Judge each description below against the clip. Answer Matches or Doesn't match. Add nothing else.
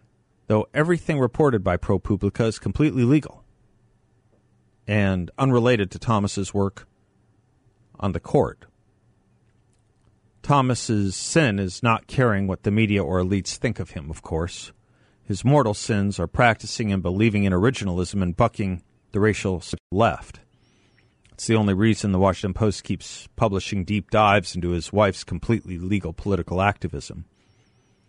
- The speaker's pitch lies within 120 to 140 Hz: Doesn't match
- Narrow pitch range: Doesn't match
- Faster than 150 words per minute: Doesn't match